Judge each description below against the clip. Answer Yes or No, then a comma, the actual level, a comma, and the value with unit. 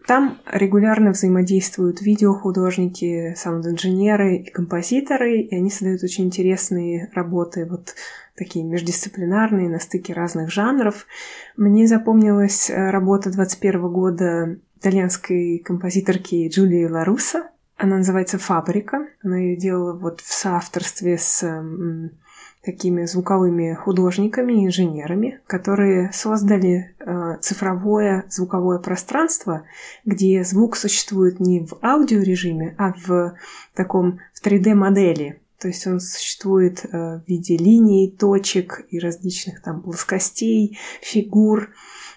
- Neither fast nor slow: No, slow, 100 wpm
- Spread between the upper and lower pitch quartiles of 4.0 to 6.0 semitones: No, narrow, 2.5 semitones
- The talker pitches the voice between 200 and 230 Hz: No, medium, 185 Hz